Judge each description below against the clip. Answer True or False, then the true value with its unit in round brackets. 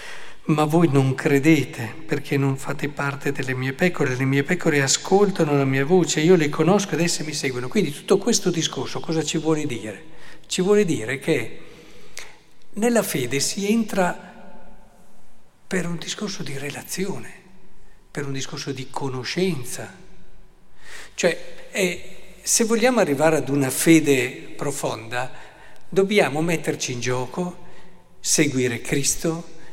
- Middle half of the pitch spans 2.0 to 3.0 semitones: False (4.7 semitones)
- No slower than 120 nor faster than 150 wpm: True (135 wpm)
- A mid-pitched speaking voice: True (160 Hz)